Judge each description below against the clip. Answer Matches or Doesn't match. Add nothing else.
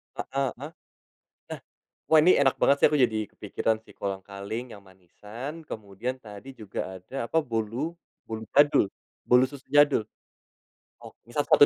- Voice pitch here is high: Doesn't match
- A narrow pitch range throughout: Doesn't match